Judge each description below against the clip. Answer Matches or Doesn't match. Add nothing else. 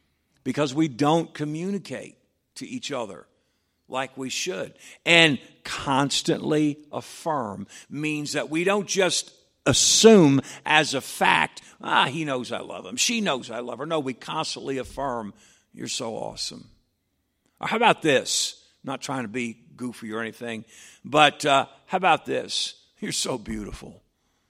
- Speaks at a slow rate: Doesn't match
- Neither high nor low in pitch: Matches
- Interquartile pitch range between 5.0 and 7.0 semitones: Doesn't match